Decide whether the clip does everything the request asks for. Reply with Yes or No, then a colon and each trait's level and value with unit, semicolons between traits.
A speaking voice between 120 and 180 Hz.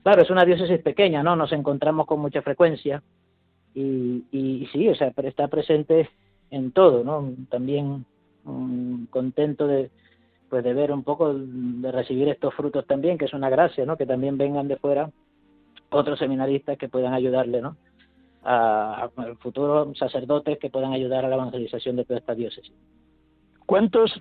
Yes: low, 135 Hz